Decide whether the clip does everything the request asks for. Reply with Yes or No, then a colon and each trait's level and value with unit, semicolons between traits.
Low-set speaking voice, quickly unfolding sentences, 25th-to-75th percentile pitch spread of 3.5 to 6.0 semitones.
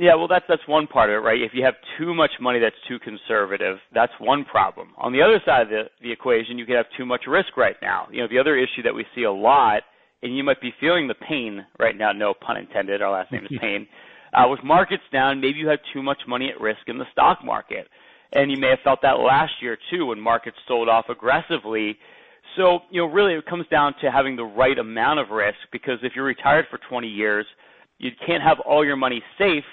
Yes: low, 130 Hz; fast, 245 wpm; average, 4.6 semitones